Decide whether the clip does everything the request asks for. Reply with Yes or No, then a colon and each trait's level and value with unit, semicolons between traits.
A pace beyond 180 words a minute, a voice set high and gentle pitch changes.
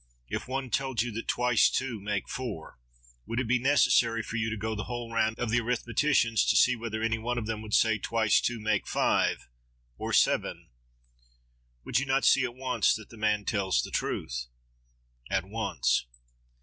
No: average, 190 wpm; low, 115 Hz; narrow, 2.3 semitones